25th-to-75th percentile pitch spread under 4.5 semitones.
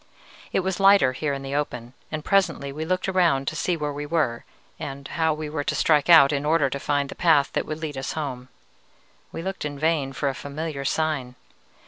Yes: average, 2.8 semitones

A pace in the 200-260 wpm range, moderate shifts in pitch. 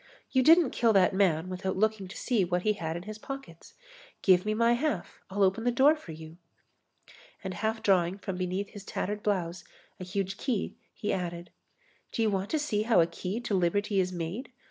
Yes: fast, 205 wpm; average, 3.3 semitones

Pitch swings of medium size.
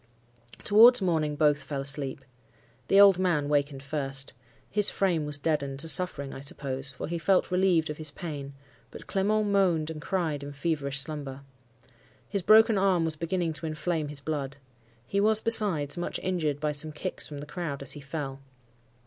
Yes: average, 4.3 semitones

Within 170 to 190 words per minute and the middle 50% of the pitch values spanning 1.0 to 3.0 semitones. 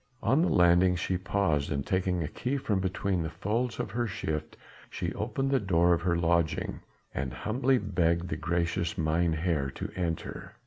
No: average, 175 wpm; average, 3.5 semitones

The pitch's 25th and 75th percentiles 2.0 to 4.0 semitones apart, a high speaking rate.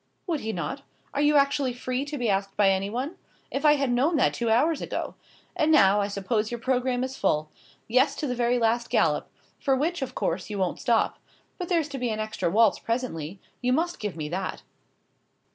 No: average, 5.2 semitones; fast, 210 wpm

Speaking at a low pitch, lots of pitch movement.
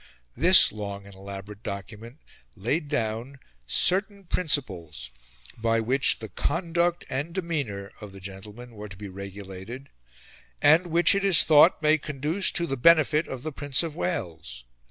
Yes: low, 130 Hz; wide, 8.2 semitones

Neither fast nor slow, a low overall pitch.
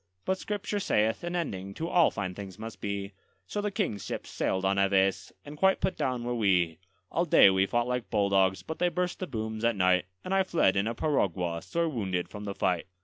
No: fast, 220 wpm; low, 110 Hz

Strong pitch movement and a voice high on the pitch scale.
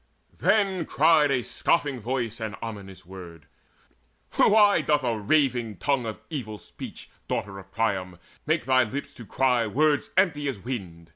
No: wide, 6.0 semitones; low, 125 Hz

